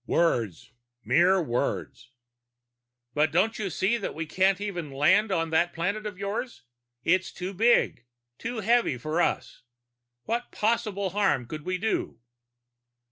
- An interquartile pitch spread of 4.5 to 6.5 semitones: Yes, average, 4.8 semitones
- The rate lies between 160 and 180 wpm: No, slow, 135 wpm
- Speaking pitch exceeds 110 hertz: Yes, medium, 185 Hz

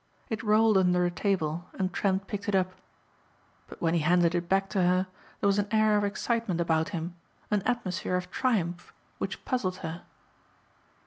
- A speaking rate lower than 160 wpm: No, average, 180 wpm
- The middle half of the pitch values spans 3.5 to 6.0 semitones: No, average, 3.0 semitones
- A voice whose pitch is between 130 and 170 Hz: No, medium, 185 Hz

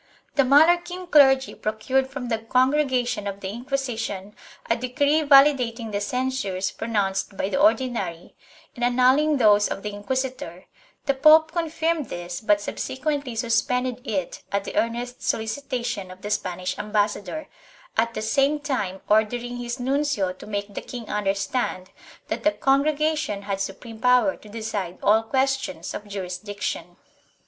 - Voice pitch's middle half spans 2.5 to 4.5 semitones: No, average, 4.9 semitones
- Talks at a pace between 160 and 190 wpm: No, average, 145 wpm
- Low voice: No, high, 240 Hz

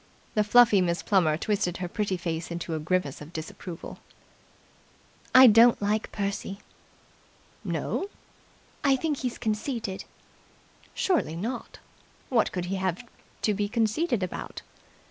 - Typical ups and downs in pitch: Yes, average, 4.7 semitones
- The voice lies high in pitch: Yes, high, 200 Hz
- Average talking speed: No, slow, 125 wpm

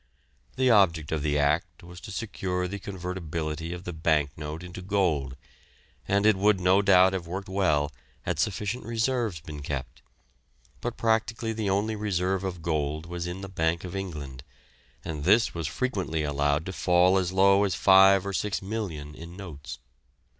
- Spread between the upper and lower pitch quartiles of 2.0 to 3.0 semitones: No, average, 3.9 semitones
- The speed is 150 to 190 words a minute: Yes, average, 170 wpm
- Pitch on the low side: Yes, very low, 90 Hz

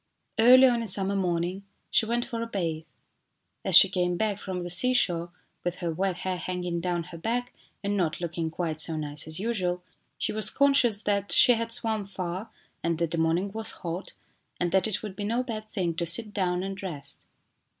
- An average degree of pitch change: Yes, average, 4.1 semitones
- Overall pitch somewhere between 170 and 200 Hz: Yes, medium, 185 Hz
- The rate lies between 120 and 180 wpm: No, average, 200 wpm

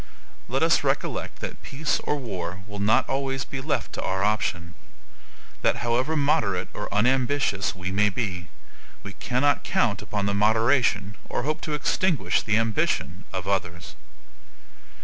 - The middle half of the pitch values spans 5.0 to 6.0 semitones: Yes, wide, 5.5 semitones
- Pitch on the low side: Yes, low, 110 Hz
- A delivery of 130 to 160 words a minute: Yes, average, 150 wpm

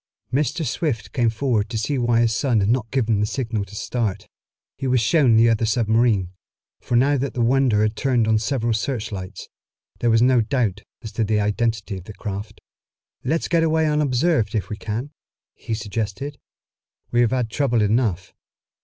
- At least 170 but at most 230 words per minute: Yes, average, 180 wpm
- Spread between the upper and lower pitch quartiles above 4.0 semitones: No, average, 3.4 semitones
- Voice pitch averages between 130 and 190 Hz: No, low, 115 Hz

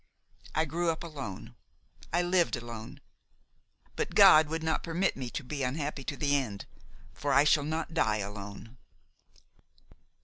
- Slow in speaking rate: No, average, 145 wpm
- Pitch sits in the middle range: Yes, medium, 145 Hz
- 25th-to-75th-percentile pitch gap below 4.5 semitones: No, average, 4.9 semitones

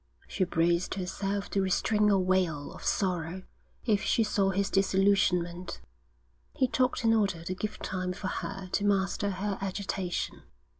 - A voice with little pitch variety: Yes, narrow, 1.8 semitones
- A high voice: Yes, high, 195 Hz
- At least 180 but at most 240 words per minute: No, average, 150 wpm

